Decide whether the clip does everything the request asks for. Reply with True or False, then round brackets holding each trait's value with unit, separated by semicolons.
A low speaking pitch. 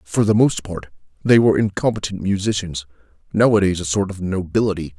True (100 Hz)